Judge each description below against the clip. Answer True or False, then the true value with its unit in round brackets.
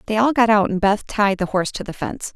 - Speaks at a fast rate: True (305 wpm)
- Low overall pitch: False (205 Hz)